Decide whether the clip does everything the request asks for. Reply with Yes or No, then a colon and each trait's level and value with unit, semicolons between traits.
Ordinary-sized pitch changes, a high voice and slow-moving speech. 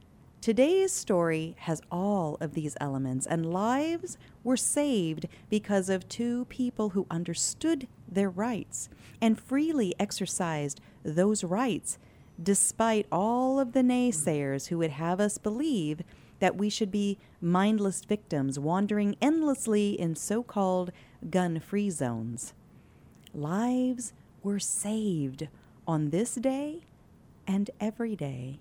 No: wide, 5.9 semitones; high, 200 Hz; slow, 120 wpm